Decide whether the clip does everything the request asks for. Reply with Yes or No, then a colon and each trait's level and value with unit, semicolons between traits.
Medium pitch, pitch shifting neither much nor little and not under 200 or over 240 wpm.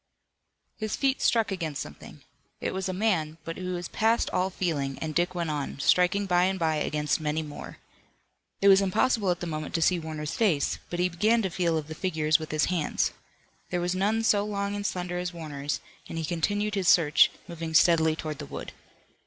Yes: medium, 175 Hz; average, 3.5 semitones; fast, 205 wpm